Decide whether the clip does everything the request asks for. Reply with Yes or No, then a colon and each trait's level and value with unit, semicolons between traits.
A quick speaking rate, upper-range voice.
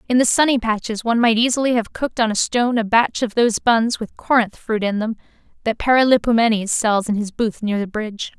Yes: fast, 220 wpm; high, 225 Hz